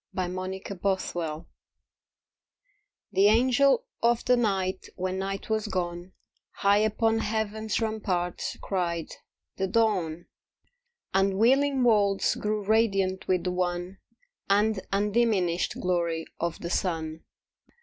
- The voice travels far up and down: No, average, 3.3 semitones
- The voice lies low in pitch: No, high, 195 Hz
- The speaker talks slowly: Yes, slow, 110 wpm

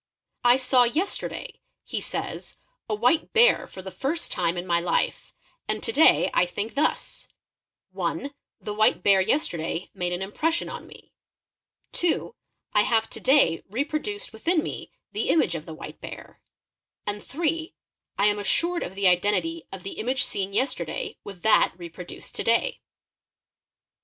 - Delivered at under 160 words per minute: No, average, 170 wpm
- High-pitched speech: Yes, high, 220 Hz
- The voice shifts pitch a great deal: Yes, wide, 8.4 semitones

